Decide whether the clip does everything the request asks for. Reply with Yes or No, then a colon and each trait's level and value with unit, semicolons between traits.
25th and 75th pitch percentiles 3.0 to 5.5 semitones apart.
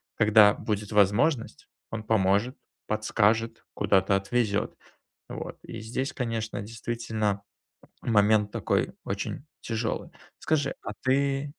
No: narrow, 2.4 semitones